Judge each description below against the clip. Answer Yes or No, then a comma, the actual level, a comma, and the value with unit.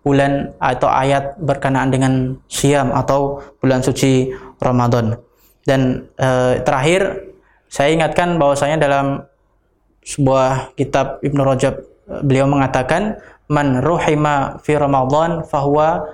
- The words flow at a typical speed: Yes, average, 105 wpm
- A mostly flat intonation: Yes, narrow, 2.1 semitones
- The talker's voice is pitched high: No, medium, 140 Hz